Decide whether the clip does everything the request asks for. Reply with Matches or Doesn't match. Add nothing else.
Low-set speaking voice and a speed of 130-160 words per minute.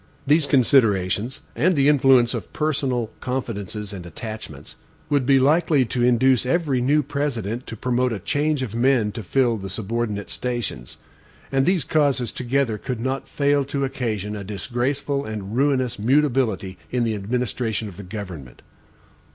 Matches